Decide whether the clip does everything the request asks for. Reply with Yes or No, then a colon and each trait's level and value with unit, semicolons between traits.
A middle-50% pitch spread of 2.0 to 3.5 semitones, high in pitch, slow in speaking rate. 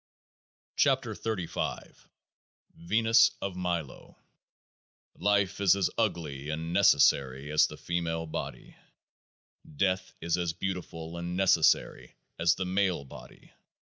No: average, 2.8 semitones; very low, 85 Hz; slow, 110 wpm